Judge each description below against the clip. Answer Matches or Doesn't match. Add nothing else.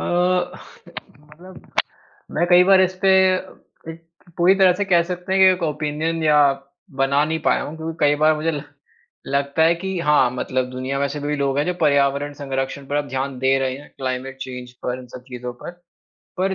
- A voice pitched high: Doesn't match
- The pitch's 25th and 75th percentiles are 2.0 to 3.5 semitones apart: Doesn't match